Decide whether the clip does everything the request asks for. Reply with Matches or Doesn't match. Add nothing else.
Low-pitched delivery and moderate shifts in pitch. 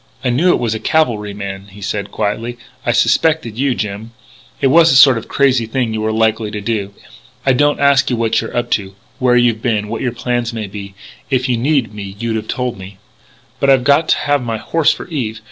Matches